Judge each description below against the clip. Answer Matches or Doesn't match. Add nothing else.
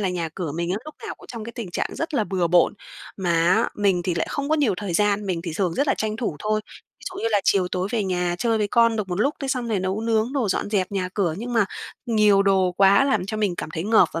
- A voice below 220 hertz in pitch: Matches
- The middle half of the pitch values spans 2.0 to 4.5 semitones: Matches